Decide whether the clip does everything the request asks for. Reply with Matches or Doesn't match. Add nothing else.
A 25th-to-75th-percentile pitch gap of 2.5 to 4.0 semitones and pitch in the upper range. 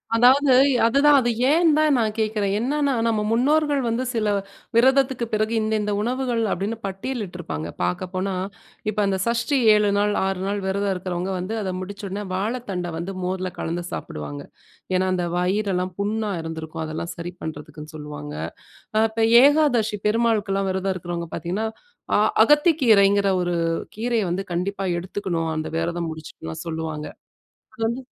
Doesn't match